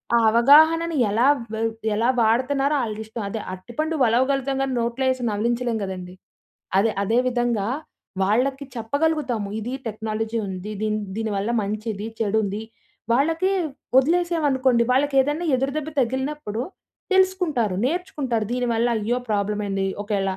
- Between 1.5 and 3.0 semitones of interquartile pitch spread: No, average, 4.3 semitones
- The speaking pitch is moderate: No, high, 240 Hz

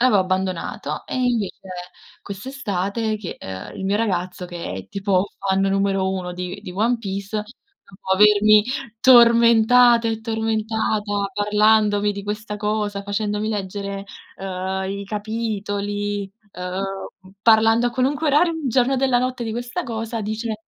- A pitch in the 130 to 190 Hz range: No, high, 210 Hz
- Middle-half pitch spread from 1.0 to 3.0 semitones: Yes, narrow, 2.6 semitones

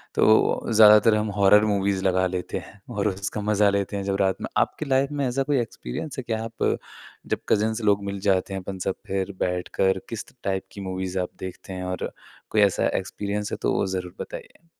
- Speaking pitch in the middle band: No, low, 100 Hz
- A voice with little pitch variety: Yes, narrow, 2.2 semitones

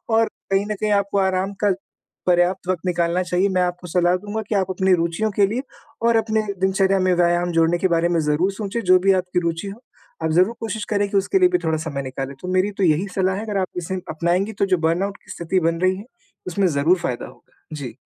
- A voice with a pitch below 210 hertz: Yes, medium, 185 Hz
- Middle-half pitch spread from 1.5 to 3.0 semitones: Yes, narrow, 2.6 semitones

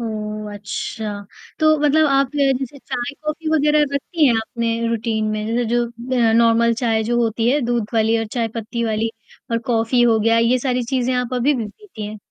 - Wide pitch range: No, narrow, 2.5 semitones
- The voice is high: Yes, high, 235 Hz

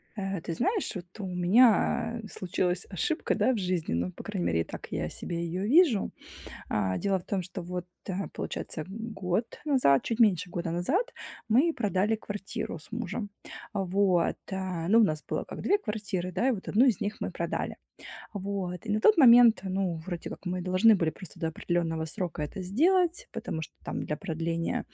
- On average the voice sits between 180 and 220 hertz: Yes, high, 190 Hz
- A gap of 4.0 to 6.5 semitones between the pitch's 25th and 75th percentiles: Yes, average, 4.3 semitones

